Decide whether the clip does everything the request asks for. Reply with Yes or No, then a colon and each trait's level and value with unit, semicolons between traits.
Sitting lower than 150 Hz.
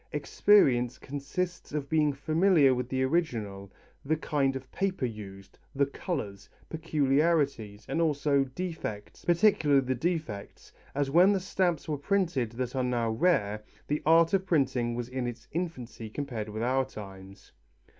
Yes: medium, 140 Hz